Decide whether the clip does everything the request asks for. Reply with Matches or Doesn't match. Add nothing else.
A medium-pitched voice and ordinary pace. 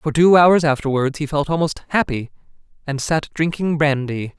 Matches